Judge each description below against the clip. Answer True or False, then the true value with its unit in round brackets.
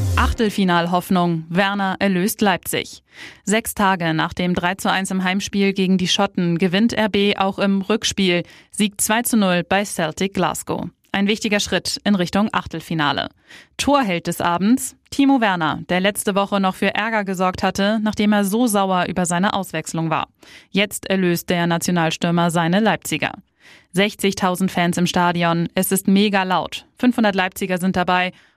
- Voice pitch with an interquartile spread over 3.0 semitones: False (2.6 semitones)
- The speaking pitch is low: False (190 Hz)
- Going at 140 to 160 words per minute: True (145 wpm)